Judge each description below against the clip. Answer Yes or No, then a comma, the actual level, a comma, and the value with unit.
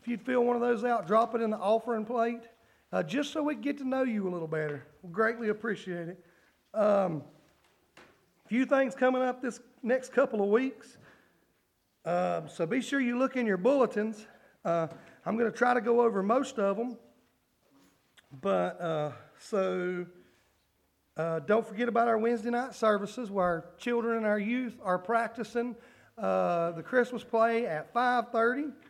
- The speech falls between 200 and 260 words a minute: No, average, 180 wpm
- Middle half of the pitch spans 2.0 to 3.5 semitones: No, average, 5.1 semitones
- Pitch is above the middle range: Yes, high, 225 Hz